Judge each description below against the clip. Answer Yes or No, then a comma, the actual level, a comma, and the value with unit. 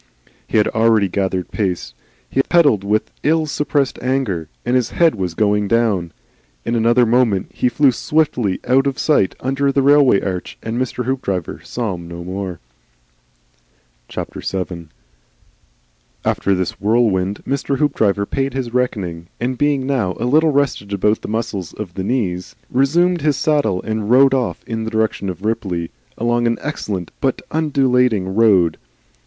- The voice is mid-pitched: No, low, 115 Hz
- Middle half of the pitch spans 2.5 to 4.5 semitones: No, wide, 5.6 semitones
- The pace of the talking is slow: No, average, 155 wpm